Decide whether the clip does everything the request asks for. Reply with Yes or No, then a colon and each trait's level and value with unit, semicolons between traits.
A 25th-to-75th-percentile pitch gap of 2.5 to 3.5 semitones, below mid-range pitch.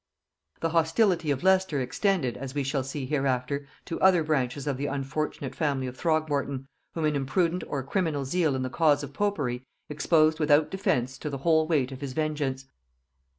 No: average, 3.1 semitones; medium, 145 Hz